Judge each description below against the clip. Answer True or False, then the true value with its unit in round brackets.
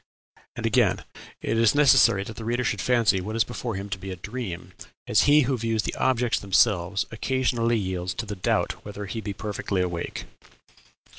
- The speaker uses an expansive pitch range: False (3.6 semitones)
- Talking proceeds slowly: False (190 wpm)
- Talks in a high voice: False (110 Hz)